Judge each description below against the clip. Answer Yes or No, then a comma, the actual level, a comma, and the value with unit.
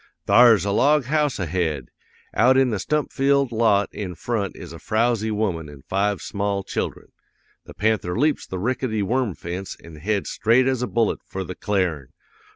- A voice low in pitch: Yes, low, 105 Hz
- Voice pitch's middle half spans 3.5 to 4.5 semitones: No, average, 4.9 semitones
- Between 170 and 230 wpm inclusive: Yes, average, 175 wpm